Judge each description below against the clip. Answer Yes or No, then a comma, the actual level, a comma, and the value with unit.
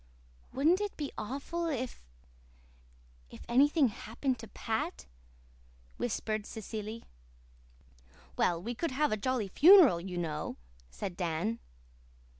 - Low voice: No, high, 230 Hz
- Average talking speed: No, slow, 110 wpm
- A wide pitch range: Yes, wide, 6.0 semitones